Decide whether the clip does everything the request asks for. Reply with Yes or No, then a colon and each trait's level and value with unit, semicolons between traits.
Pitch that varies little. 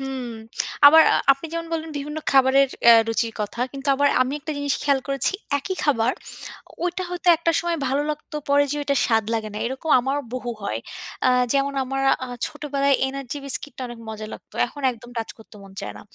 No: average, 3.1 semitones